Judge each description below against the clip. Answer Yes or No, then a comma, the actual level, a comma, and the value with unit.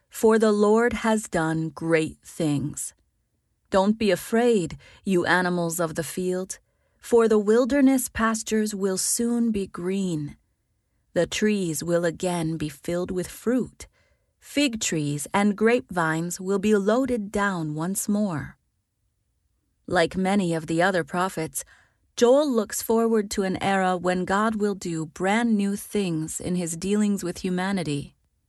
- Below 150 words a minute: Yes, slow, 135 wpm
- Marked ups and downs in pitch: No, average, 4.6 semitones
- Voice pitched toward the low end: No, medium, 185 Hz